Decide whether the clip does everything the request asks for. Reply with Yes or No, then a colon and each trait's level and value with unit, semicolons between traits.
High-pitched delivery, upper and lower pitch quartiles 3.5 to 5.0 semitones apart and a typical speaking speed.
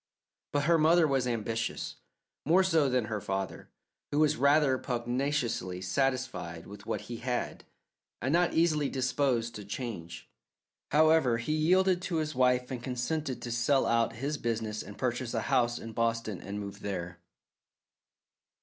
No: low, 125 Hz; average, 4.4 semitones; average, 150 wpm